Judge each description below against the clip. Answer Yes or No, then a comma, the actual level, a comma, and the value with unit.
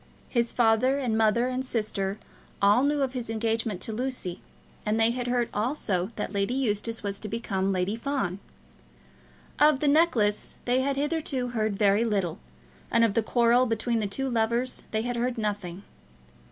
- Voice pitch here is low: No, high, 230 Hz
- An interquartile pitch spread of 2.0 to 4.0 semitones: Yes, average, 3.3 semitones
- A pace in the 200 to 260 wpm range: No, average, 170 wpm